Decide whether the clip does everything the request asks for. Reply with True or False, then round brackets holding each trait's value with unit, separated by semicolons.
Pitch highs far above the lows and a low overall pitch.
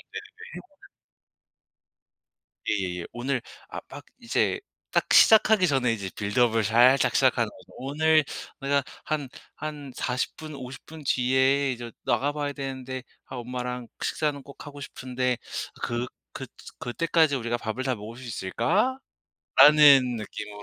False (3.4 semitones; 130 Hz)